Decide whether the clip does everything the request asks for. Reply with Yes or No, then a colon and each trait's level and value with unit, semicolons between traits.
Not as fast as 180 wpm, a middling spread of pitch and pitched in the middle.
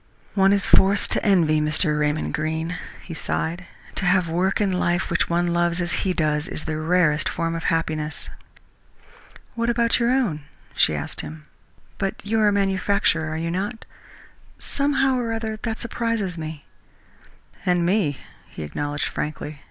Yes: average, 165 wpm; average, 4.4 semitones; medium, 175 Hz